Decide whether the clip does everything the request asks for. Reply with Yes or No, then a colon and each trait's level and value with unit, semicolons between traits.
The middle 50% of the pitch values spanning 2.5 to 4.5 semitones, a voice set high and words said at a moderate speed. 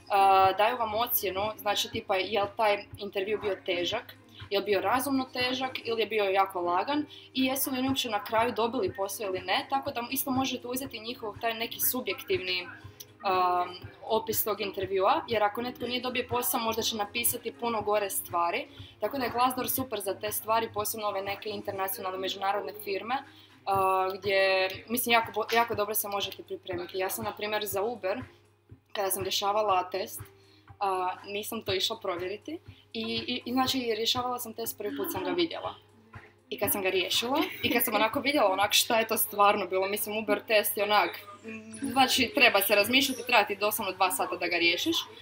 No: average, 3.7 semitones; high, 210 Hz; fast, 185 wpm